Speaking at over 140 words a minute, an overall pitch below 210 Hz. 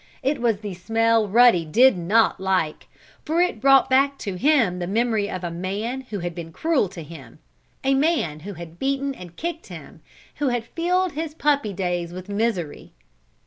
No: average, 185 wpm; high, 220 Hz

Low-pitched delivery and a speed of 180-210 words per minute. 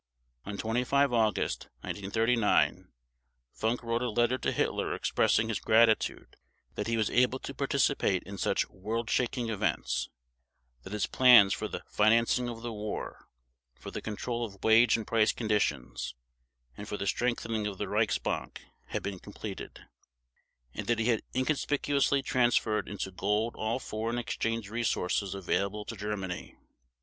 No: low, 115 Hz; average, 145 wpm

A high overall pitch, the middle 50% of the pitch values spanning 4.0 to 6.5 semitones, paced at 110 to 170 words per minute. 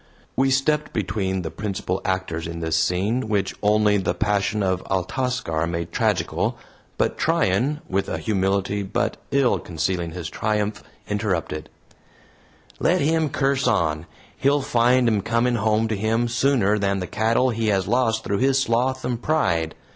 No: low, 105 Hz; average, 4.8 semitones; average, 155 wpm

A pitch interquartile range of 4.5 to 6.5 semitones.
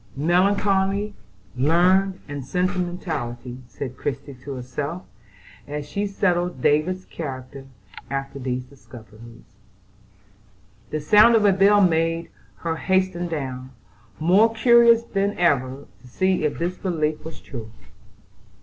Yes: wide, 5.6 semitones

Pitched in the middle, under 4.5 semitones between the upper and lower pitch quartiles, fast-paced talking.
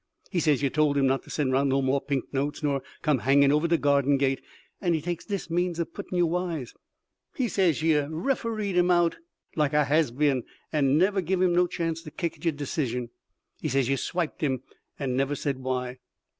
Yes: medium, 150 Hz; average, 4.0 semitones; fast, 215 wpm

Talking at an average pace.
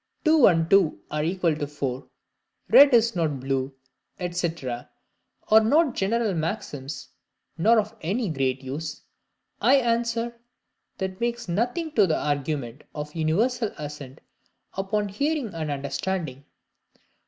No: slow, 125 wpm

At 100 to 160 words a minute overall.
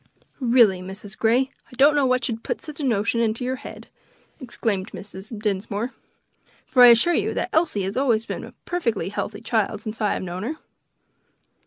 No: average, 180 wpm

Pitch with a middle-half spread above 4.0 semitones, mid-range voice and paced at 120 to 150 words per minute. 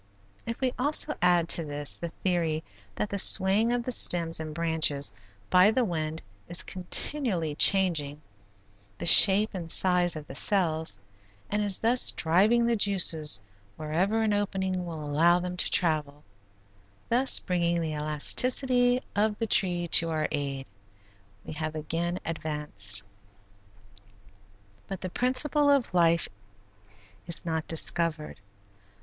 Yes: average, 4.7 semitones; medium, 175 Hz; slow, 135 wpm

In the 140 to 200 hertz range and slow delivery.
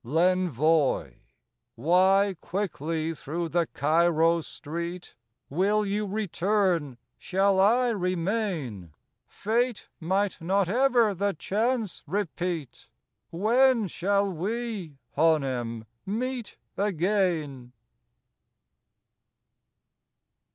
Yes: medium, 185 Hz; slow, 80 wpm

